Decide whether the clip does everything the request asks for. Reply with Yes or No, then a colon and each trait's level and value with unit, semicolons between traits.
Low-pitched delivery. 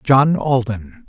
Yes: low, 130 Hz